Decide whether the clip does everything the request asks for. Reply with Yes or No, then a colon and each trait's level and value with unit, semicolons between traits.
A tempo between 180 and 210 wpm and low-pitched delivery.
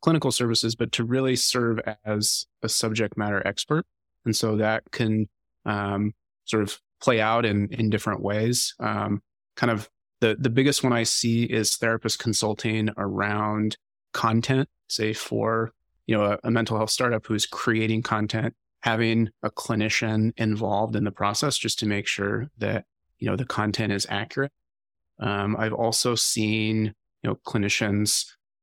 No: average, 155 wpm; low, 110 Hz